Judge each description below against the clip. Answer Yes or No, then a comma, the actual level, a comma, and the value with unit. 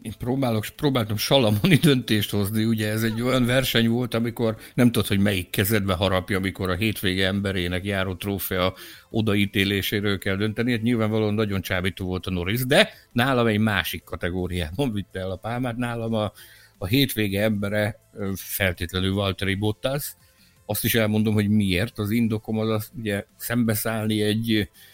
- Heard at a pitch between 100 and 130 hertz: Yes, low, 105 Hz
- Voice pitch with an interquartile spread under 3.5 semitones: Yes, average, 2.9 semitones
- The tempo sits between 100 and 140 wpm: No, fast, 155 wpm